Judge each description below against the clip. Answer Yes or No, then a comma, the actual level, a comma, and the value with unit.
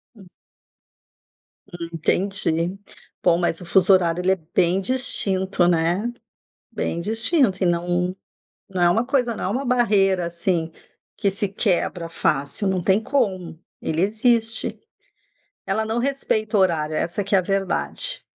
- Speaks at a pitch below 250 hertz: Yes, high, 190 Hz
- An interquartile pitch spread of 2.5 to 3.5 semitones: No, average, 3.9 semitones